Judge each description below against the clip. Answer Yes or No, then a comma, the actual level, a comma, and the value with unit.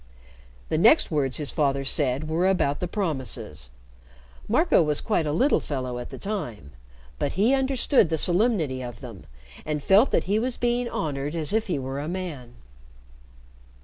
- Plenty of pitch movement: Yes, wide, 7.3 semitones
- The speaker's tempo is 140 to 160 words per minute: No, average, 170 wpm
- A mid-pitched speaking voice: Yes, medium, 155 Hz